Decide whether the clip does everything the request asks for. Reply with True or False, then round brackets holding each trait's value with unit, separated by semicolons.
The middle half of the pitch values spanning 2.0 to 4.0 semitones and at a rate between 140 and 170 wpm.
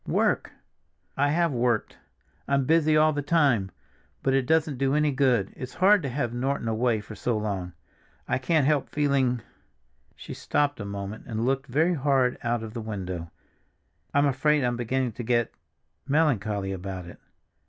False (4.6 semitones; 165 wpm)